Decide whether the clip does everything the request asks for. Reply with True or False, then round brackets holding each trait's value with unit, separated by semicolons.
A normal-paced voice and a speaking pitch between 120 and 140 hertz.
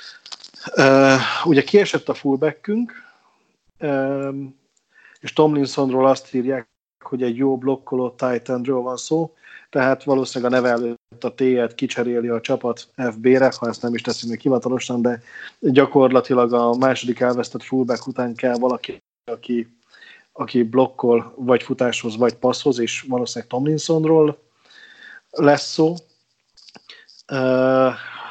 True (120 wpm; 130 Hz)